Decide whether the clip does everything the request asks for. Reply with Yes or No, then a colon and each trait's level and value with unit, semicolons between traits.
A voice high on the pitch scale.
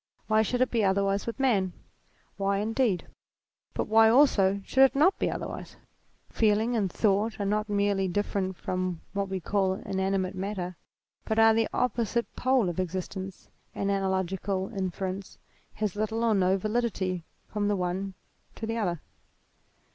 Yes: high, 200 Hz